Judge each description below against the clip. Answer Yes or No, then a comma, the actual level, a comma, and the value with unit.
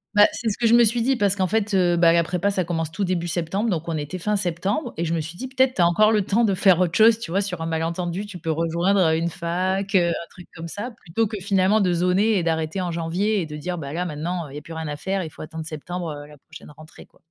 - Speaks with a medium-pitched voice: Yes, medium, 180 Hz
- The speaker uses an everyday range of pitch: Yes, average, 3.5 semitones